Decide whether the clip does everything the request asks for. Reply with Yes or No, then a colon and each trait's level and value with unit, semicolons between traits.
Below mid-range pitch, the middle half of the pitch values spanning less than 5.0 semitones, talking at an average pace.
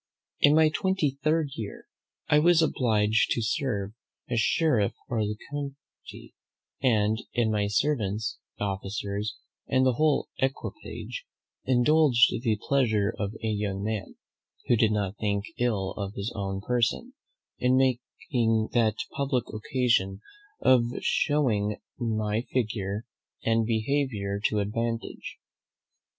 No: low, 115 Hz; average, 4.0 semitones; slow, 120 wpm